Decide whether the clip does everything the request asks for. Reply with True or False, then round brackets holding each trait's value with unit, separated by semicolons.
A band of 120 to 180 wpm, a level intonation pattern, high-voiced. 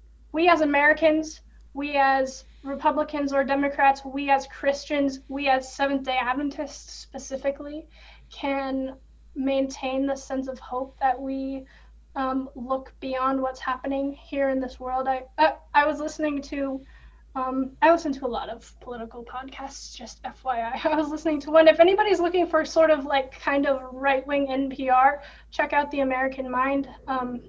True (155 wpm; 1.8 semitones; 275 Hz)